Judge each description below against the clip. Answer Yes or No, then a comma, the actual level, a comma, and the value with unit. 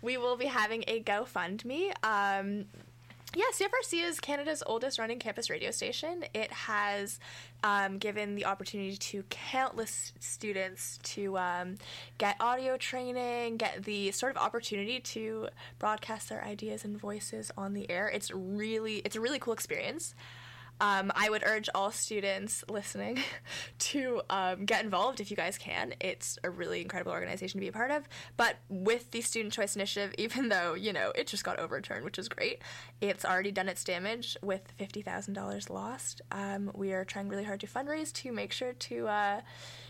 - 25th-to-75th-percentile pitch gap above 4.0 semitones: No, average, 3.5 semitones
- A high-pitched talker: Yes, high, 205 Hz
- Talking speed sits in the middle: Yes, average, 175 wpm